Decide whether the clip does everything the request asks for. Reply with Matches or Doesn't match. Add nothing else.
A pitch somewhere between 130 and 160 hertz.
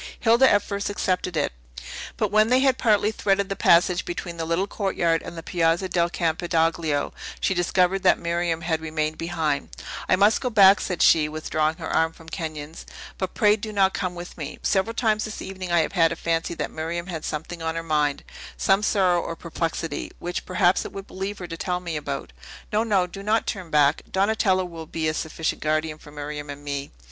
Doesn't match